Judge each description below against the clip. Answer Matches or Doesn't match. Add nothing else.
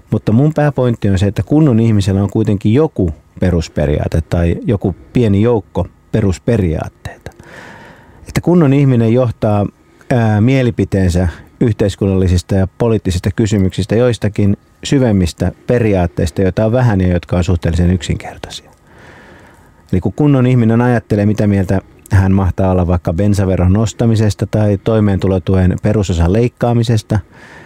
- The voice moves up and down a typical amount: Matches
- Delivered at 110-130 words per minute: Matches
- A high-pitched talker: Doesn't match